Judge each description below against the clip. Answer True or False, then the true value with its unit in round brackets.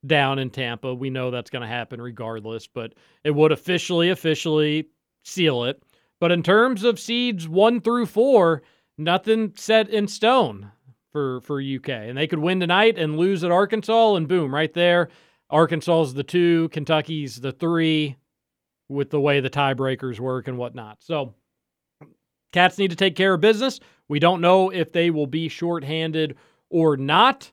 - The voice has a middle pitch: True (160 Hz)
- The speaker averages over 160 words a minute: True (170 wpm)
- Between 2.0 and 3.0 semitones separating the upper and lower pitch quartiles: False (5.0 semitones)